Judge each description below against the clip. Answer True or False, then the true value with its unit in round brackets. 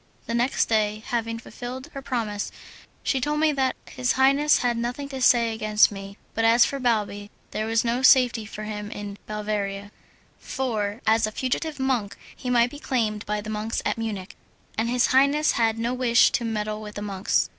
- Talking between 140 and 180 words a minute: False (190 wpm)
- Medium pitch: False (230 Hz)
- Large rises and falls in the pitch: False (3.2 semitones)